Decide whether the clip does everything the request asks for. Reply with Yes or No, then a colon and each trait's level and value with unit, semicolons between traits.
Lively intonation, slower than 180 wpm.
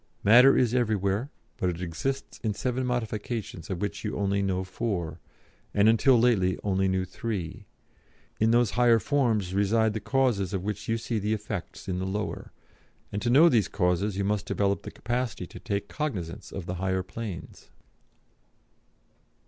No: average, 3.5 semitones; average, 165 wpm